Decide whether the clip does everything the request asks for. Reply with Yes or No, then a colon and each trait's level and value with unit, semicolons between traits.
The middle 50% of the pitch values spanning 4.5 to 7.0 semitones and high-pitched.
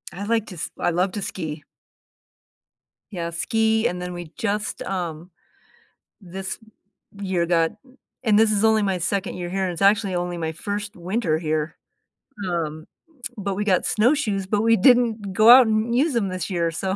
No: average, 3.8 semitones; high, 195 Hz